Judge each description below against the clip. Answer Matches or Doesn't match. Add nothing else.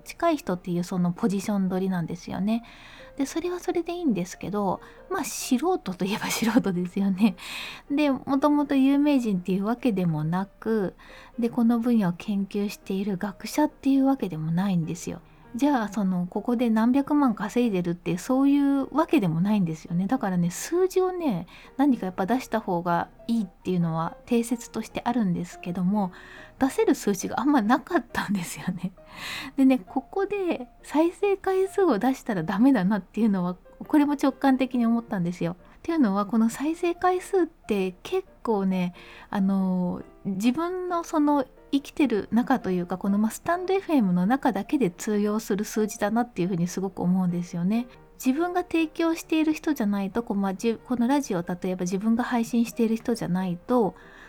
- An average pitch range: Doesn't match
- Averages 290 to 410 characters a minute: Matches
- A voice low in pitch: Doesn't match